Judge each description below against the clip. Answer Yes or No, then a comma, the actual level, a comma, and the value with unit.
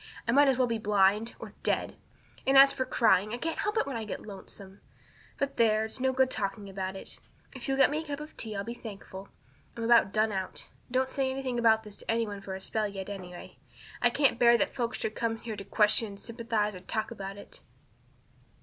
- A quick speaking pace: Yes, fast, 230 wpm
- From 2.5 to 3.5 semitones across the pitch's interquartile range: No, average, 4.1 semitones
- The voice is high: Yes, high, 225 Hz